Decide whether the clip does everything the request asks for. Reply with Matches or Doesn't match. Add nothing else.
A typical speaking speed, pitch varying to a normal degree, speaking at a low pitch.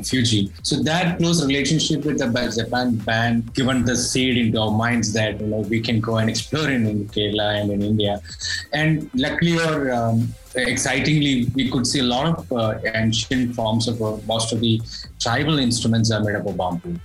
Matches